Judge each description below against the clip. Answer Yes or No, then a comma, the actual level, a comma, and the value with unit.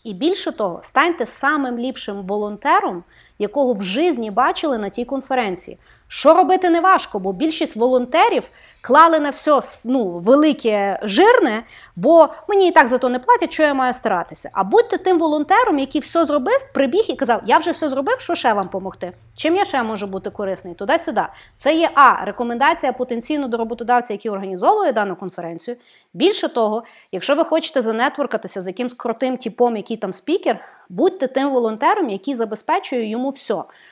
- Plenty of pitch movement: Yes, wide, 6.4 semitones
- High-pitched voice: Yes, very high, 260 Hz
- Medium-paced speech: No, fast, 170 wpm